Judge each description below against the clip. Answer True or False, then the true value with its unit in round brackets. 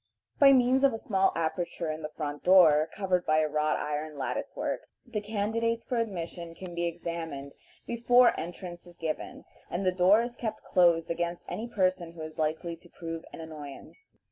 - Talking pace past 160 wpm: True (185 wpm)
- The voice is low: False (175 Hz)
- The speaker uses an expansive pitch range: False (4.7 semitones)